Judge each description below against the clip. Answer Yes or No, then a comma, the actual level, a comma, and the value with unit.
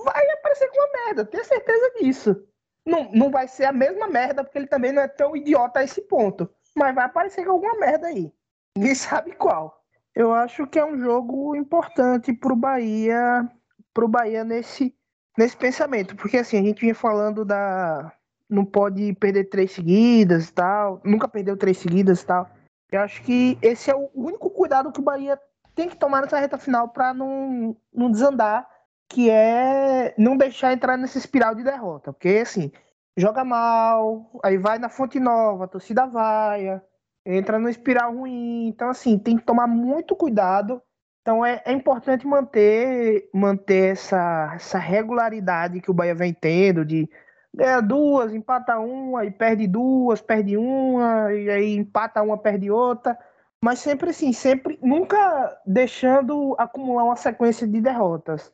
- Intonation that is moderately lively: Yes, average, 4.6 semitones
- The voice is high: Yes, high, 235 Hz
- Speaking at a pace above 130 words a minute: Yes, average, 170 wpm